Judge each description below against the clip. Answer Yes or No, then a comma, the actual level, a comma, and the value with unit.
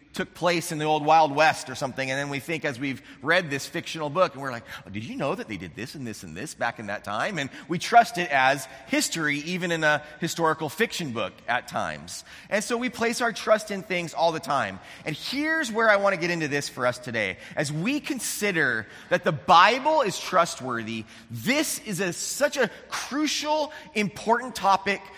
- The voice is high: No, medium, 170 Hz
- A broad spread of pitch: Yes, wide, 6.8 semitones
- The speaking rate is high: Yes, fast, 215 wpm